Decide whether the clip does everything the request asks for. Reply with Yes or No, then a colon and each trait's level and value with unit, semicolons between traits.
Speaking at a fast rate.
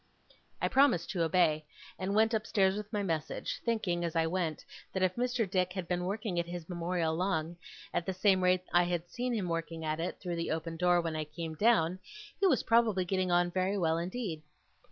Yes: fast, 215 wpm